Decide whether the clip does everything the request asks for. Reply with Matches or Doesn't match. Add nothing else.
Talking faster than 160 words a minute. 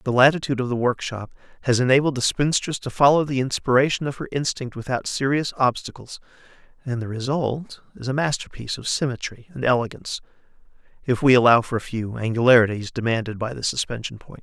Matches